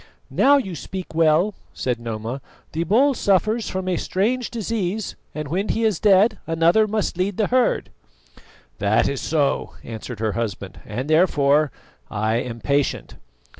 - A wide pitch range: Yes, wide, 8.2 semitones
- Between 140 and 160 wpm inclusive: Yes, average, 150 wpm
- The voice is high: No, medium, 170 Hz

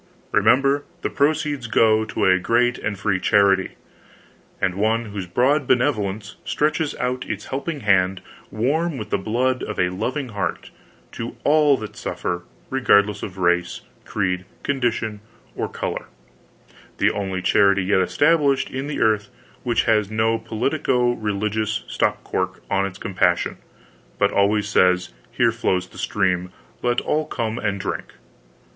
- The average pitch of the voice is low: Yes, low, 110 Hz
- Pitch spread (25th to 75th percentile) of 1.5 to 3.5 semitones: No, average, 4.6 semitones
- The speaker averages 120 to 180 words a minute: Yes, average, 145 wpm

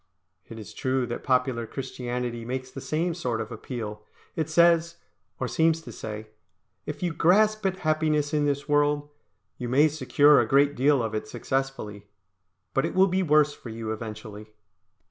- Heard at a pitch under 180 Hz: Yes, low, 135 Hz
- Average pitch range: Yes, average, 5.0 semitones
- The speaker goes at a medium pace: Yes, average, 170 wpm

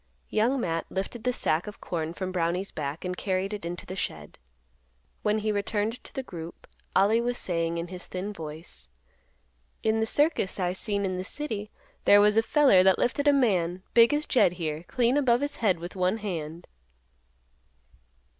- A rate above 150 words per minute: Yes, average, 185 wpm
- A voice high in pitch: Yes, high, 195 Hz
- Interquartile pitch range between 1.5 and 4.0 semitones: No, average, 4.5 semitones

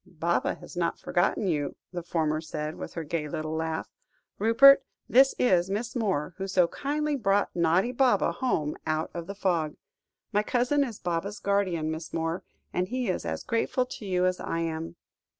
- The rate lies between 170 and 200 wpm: Yes, average, 180 wpm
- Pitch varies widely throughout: Yes, wide, 5.8 semitones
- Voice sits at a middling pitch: Yes, medium, 180 Hz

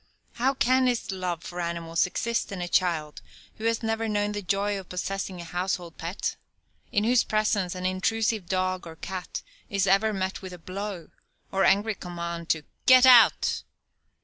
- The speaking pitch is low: No, high, 190 Hz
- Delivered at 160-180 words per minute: Yes, average, 175 wpm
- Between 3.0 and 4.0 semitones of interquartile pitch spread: Yes, average, 3.4 semitones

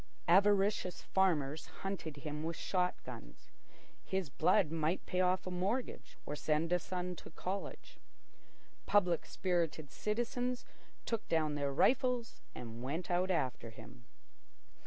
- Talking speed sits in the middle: No, slow, 130 wpm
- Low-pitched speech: No, medium, 180 Hz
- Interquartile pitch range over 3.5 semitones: Yes, average, 4.1 semitones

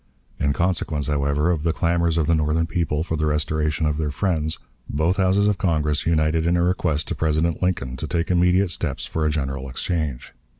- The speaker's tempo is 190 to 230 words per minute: Yes, average, 200 wpm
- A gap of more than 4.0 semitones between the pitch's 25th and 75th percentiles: No, narrow, 2.5 semitones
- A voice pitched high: No, very low, 80 Hz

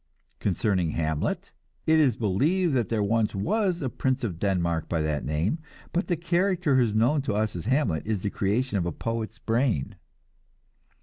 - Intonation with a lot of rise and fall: Yes, wide, 7.3 semitones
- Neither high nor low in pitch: No, low, 110 Hz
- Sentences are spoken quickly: No, average, 175 wpm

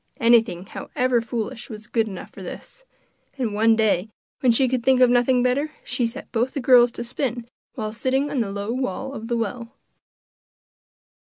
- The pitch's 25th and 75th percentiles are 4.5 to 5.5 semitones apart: No, narrow, 2.4 semitones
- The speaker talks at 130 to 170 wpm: No, average, 180 wpm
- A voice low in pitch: No, high, 240 Hz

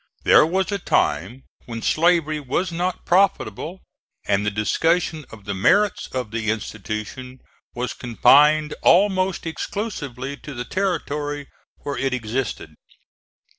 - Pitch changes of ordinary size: No, wide, 7.0 semitones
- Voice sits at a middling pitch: Yes, medium, 145 Hz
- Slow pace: Yes, slow, 125 wpm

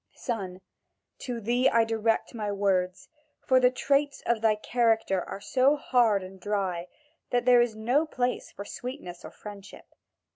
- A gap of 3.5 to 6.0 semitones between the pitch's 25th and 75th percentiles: Yes, average, 3.8 semitones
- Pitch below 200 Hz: No, high, 225 Hz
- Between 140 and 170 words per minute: Yes, average, 155 wpm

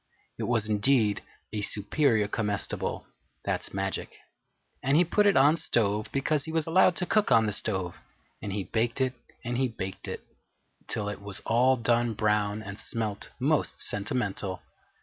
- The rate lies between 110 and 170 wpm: Yes, average, 165 wpm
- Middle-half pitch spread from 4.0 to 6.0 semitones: Yes, average, 4.4 semitones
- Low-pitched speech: Yes, low, 110 Hz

